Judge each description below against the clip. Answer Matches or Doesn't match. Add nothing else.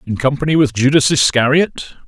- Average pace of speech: Matches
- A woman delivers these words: Doesn't match